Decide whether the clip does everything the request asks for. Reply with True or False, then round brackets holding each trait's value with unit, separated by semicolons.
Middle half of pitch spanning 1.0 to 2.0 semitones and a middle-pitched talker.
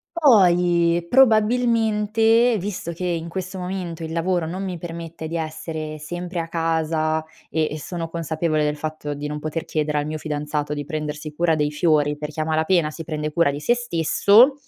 False (2.9 semitones; 165 Hz)